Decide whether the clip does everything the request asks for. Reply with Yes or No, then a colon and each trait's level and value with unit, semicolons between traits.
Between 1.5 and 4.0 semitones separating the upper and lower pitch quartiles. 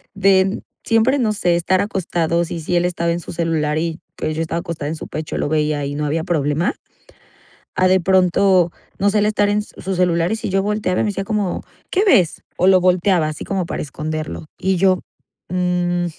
Yes: average, 2.9 semitones